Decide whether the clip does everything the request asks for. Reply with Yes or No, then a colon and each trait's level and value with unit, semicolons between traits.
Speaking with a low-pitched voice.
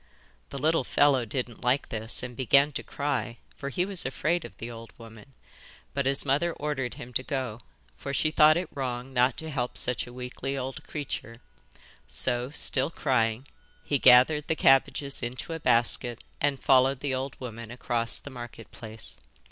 Yes: low, 130 Hz